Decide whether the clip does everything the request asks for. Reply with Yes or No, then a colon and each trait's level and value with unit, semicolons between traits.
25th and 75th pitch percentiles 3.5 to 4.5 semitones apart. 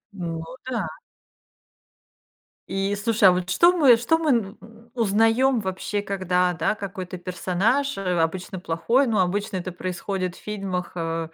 Yes: average, 3.8 semitones